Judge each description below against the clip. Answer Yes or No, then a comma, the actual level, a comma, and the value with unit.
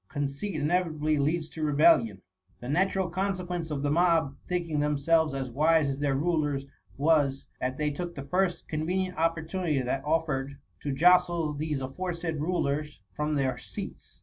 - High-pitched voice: No, medium, 155 Hz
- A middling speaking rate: Yes, average, 160 wpm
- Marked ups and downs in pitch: No, average, 3.4 semitones